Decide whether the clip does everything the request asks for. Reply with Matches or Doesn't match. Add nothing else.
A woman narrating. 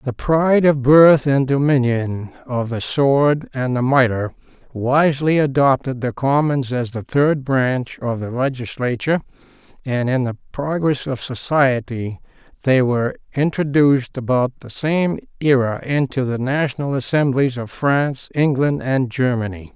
Doesn't match